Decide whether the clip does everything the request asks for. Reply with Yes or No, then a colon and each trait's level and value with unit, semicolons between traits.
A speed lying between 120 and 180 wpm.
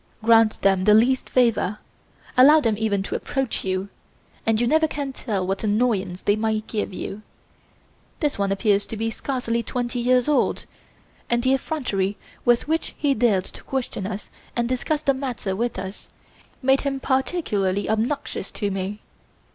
Yes: average, 165 wpm